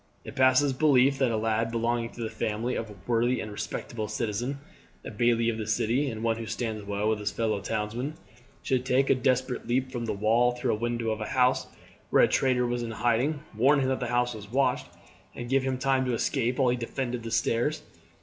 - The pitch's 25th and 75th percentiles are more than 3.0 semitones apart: No, narrow, 2.4 semitones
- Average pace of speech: No, fast, 225 wpm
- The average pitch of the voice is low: Yes, low, 120 Hz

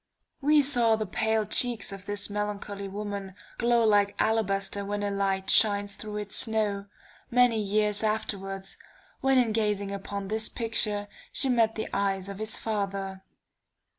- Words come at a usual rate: Yes, average, 150 wpm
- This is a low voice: No, high, 210 Hz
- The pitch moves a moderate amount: No, narrow, 1.9 semitones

